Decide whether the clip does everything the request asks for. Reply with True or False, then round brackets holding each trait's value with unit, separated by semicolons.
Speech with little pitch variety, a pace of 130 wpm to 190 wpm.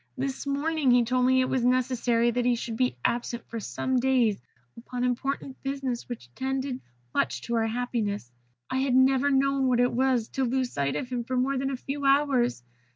False (1.9 semitones; 205 wpm)